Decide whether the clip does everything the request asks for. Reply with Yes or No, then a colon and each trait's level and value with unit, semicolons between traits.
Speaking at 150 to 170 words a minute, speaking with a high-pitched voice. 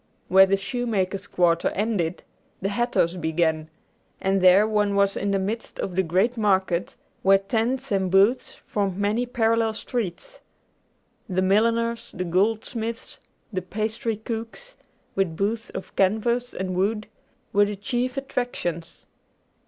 No: slow, 135 wpm; high, 200 Hz